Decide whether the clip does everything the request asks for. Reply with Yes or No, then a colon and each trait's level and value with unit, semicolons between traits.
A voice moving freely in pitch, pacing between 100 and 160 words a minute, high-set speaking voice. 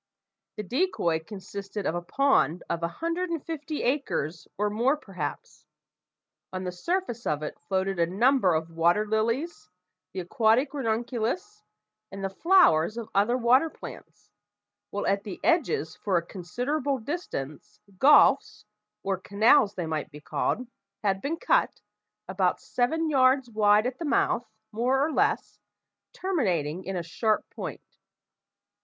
Yes: wide, 7.2 semitones; average, 145 wpm; high, 220 Hz